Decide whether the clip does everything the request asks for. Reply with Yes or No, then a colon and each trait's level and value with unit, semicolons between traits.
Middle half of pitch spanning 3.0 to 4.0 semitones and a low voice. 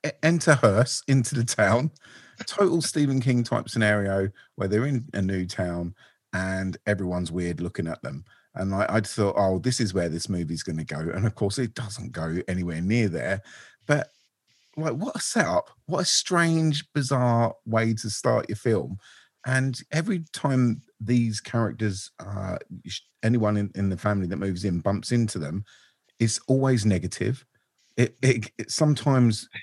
No: average, 5.1 semitones; low, 110 Hz